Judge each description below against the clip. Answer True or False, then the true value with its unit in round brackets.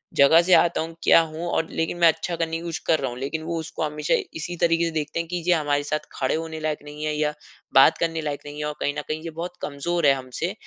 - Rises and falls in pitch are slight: True (2.0 semitones)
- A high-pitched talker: False (160 Hz)